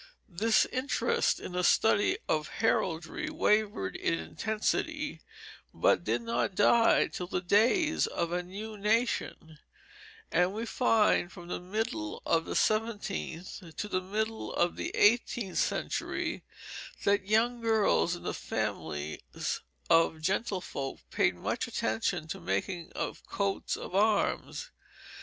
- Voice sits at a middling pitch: No, high, 200 Hz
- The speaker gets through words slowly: Yes, slow, 130 wpm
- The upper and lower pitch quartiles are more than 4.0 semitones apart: Yes, average, 4.4 semitones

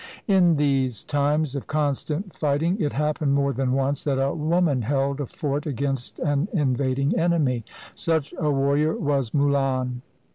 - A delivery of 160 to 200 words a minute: No, average, 150 wpm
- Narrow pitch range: Yes, narrow, 2.1 semitones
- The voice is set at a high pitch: No, medium, 140 Hz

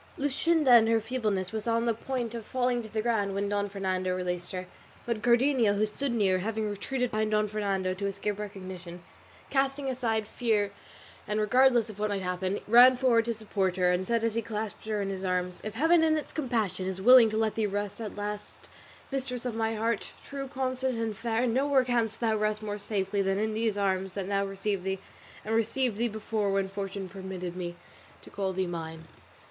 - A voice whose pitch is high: Yes, high, 215 Hz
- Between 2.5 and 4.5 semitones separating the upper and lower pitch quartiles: Yes, average, 3.3 semitones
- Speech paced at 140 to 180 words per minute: No, fast, 205 wpm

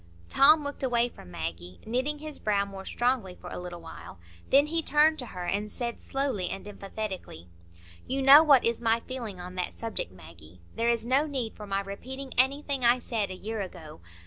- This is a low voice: No, high, 225 Hz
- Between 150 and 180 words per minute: No, average, 200 wpm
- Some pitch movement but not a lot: No, wide, 6.4 semitones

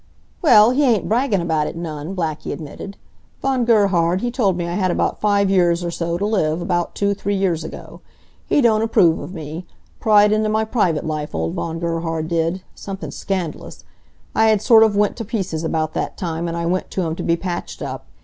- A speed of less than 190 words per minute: No, fast, 205 wpm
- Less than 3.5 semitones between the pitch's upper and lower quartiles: No, average, 4.1 semitones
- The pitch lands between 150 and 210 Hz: Yes, medium, 185 Hz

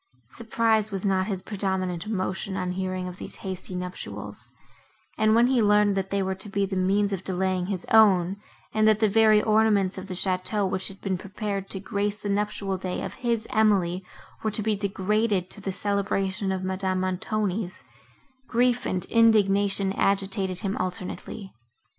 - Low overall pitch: No, high, 195 Hz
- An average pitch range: No, narrow, 2.1 semitones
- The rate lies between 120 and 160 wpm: No, average, 170 wpm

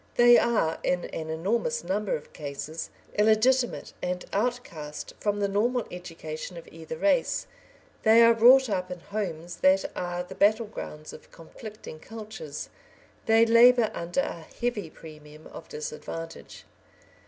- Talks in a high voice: Yes, high, 195 Hz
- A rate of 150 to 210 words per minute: No, average, 140 wpm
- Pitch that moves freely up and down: Yes, wide, 5.9 semitones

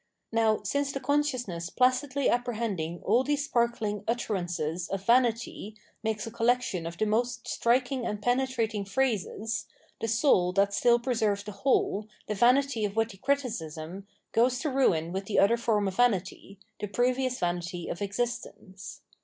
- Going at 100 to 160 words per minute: Yes, average, 150 wpm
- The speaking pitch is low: No, high, 225 Hz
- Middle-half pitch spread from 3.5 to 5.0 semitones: Yes, average, 3.9 semitones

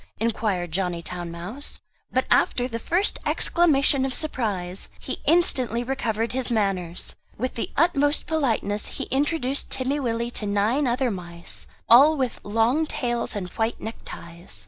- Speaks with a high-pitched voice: Yes, high, 235 Hz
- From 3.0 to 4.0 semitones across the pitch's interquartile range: No, average, 5.1 semitones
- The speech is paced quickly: No, average, 145 wpm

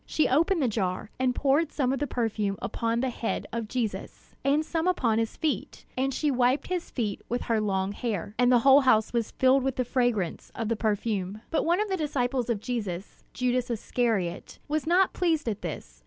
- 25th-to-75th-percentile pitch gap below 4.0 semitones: No, average, 4.3 semitones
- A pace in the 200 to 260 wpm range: Yes, fast, 205 wpm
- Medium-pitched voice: No, high, 245 Hz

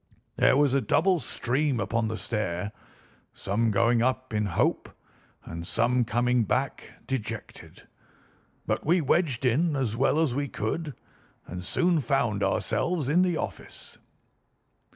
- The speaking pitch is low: Yes, low, 125 Hz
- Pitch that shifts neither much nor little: Yes, average, 4.8 semitones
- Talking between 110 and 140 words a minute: Yes, slow, 135 wpm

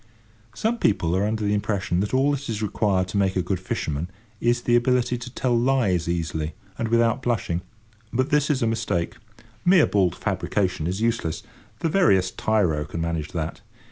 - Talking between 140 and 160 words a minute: No, average, 180 wpm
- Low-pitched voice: Yes, low, 105 Hz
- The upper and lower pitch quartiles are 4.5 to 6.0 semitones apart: Yes, wide, 5.5 semitones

